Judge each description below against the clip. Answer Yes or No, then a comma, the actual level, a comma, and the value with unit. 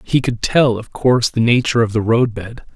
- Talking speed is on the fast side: Yes, fast, 220 wpm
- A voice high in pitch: No, low, 115 Hz